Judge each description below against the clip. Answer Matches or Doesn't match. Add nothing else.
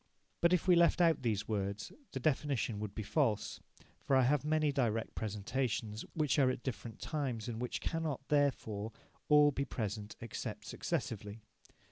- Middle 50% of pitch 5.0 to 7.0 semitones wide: Matches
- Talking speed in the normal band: Matches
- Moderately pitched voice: Doesn't match